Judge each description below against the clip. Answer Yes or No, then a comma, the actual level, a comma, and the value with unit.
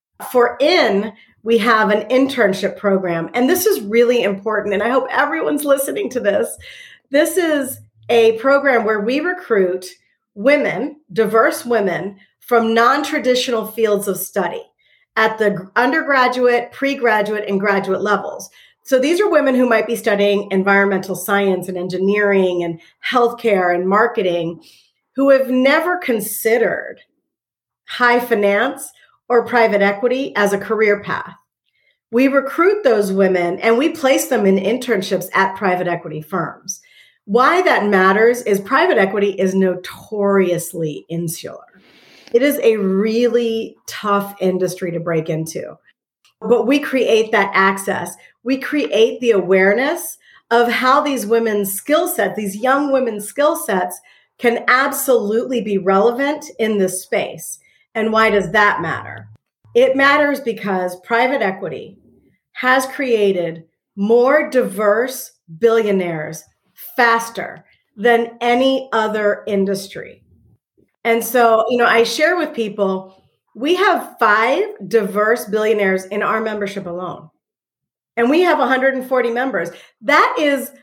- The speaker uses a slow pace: Yes, slow, 130 wpm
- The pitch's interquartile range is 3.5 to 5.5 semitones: Yes, average, 4.7 semitones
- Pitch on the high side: Yes, high, 225 Hz